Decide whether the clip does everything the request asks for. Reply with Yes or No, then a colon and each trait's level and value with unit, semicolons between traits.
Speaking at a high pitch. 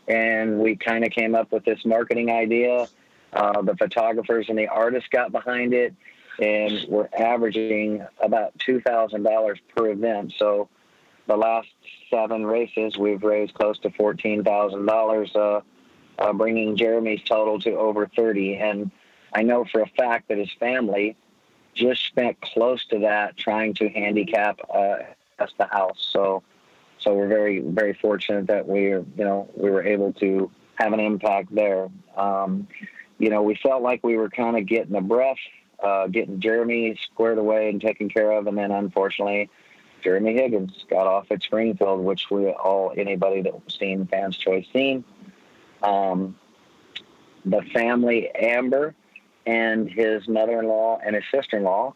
No: low, 110 Hz